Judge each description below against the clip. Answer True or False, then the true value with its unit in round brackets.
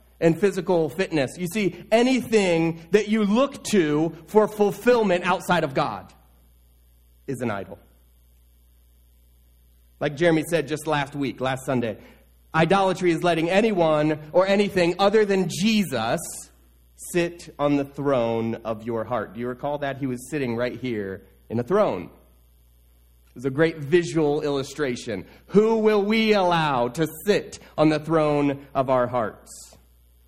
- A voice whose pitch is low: False (150 Hz)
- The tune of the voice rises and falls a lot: True (8.0 semitones)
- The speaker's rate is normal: True (145 wpm)